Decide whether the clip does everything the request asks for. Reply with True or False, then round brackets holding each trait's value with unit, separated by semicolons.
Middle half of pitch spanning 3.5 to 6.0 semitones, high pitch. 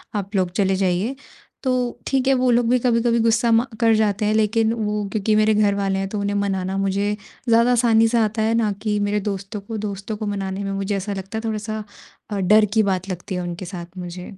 False (2.5 semitones; 210 Hz)